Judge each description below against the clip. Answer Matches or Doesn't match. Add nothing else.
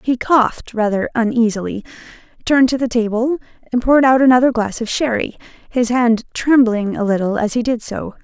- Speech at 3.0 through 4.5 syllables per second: Doesn't match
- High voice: Matches